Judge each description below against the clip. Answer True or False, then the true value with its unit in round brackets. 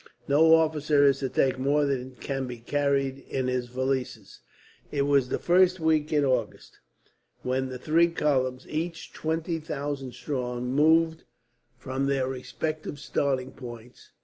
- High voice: False (140 Hz)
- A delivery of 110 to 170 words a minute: True (145 wpm)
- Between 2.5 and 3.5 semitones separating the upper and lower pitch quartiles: True (3.1 semitones)